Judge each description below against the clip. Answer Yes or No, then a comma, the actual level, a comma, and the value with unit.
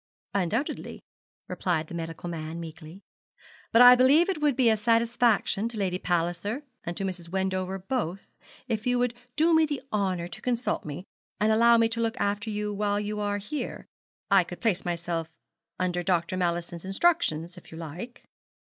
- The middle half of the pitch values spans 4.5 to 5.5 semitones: Yes, average, 5.1 semitones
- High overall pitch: Yes, high, 200 Hz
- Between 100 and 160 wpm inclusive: No, average, 175 wpm